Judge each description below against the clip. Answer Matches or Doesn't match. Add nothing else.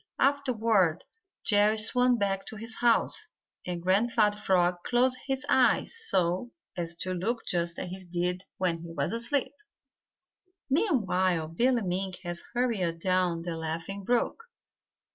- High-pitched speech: Matches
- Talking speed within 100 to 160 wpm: Matches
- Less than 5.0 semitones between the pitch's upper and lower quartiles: Doesn't match